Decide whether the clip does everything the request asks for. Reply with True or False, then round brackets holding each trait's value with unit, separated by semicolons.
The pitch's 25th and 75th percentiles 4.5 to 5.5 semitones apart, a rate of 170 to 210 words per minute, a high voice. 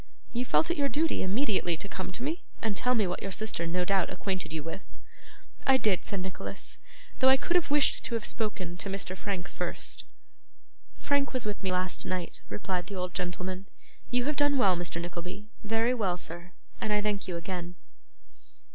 True (5.2 semitones; 195 wpm; 195 Hz)